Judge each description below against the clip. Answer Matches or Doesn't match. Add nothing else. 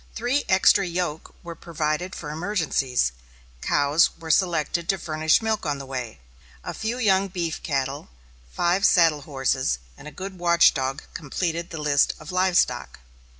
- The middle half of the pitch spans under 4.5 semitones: Matches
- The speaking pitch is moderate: Matches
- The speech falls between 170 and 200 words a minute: Doesn't match